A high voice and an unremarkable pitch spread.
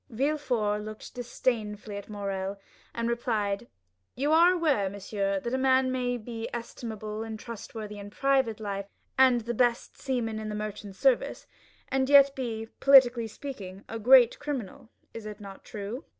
Yes: high, 230 Hz; average, 3.7 semitones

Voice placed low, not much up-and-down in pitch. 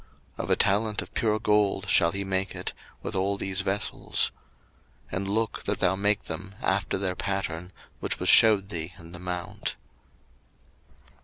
Yes: very low, 95 Hz; narrow, 2.0 semitones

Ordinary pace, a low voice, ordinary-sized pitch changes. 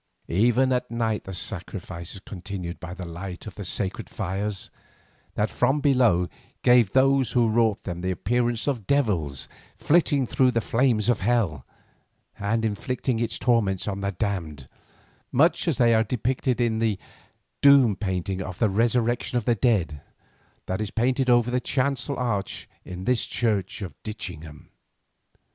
Yes: average, 150 wpm; low, 110 Hz; average, 4.5 semitones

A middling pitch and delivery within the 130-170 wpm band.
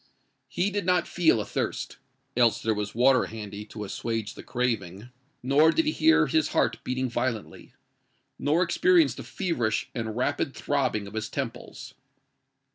No: low, 125 Hz; average, 140 wpm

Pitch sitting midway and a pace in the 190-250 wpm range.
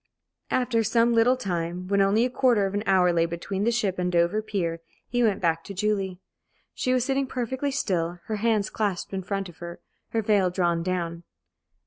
No: high, 200 Hz; average, 195 wpm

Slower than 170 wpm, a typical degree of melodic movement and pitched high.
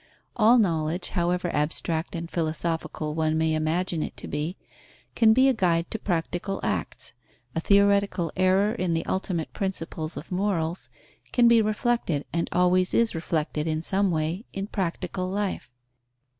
No: average, 150 wpm; average, 3.6 semitones; medium, 175 Hz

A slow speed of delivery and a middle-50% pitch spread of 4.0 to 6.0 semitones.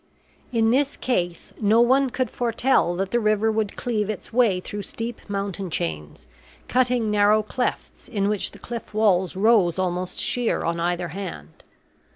No: average, 160 wpm; average, 4.4 semitones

